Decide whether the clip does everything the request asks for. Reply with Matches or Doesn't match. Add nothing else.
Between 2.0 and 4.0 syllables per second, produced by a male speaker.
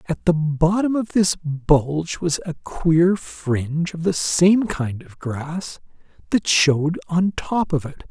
Matches